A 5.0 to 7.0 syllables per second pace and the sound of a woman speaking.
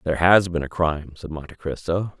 No: 5.9 syllables/s; male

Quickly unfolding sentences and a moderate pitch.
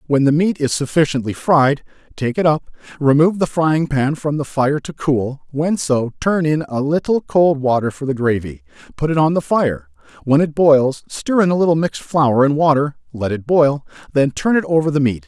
Yes: fast, 210 wpm; medium, 145 Hz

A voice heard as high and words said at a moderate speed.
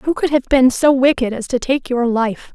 No: very high, 255 Hz; fast, 260 wpm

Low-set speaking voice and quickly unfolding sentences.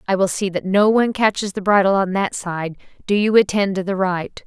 No: high, 195 Hz; fast, 240 wpm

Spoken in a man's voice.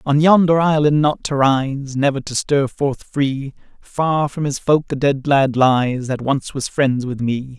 Yes: male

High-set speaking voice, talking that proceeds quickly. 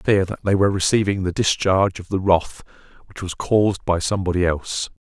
No: very low, 95 Hz; fast, 215 wpm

